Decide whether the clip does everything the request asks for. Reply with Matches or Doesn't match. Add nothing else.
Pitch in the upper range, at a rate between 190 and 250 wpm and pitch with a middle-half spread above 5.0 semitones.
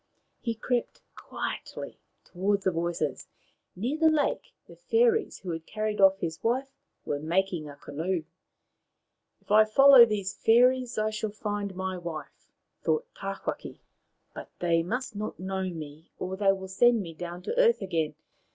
Doesn't match